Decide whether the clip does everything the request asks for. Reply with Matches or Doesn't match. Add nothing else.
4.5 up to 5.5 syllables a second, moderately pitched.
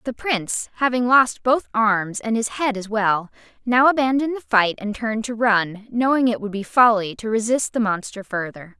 Doesn't match